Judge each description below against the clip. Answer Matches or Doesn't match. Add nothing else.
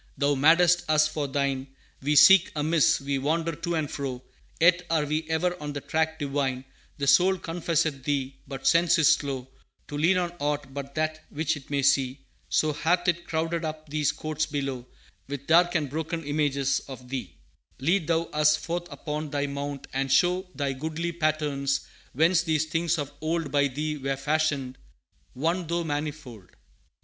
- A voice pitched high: Doesn't match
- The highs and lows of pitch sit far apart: Doesn't match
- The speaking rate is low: Doesn't match